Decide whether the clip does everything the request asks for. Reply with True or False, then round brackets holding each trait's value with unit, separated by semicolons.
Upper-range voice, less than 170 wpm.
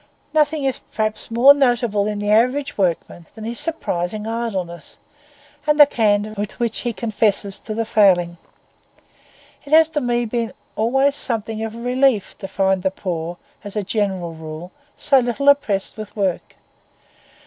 True (220 Hz; 160 wpm)